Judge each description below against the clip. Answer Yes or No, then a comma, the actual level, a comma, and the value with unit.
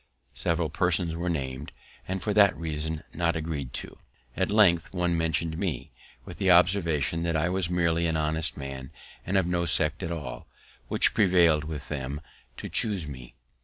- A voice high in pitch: No, very low, 85 Hz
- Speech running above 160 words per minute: Yes, average, 170 wpm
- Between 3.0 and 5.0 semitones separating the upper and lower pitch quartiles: No, narrow, 2.5 semitones